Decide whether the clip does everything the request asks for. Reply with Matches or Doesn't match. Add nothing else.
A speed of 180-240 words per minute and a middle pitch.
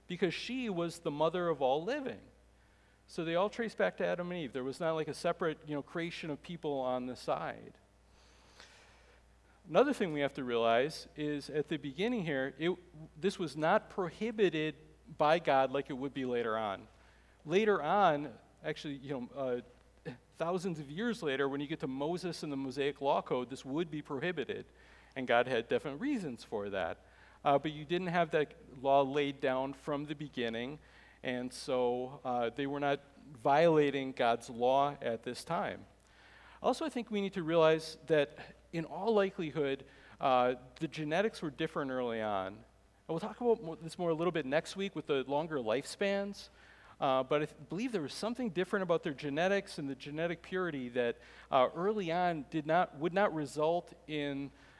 Matches